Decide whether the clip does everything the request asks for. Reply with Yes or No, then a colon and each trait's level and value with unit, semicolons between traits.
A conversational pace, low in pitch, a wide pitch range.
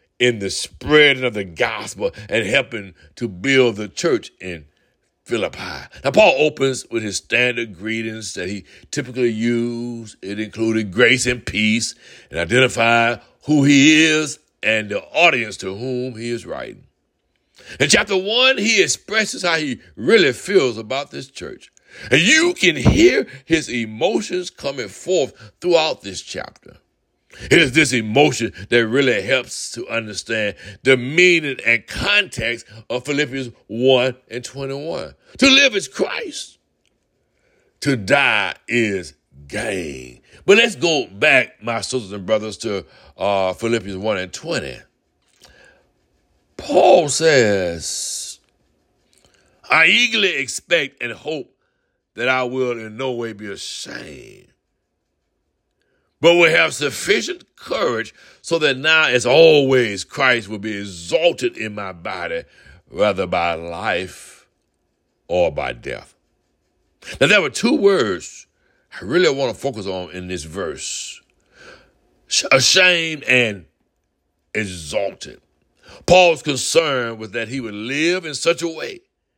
No: slow, 130 wpm; low, 125 Hz; wide, 6.8 semitones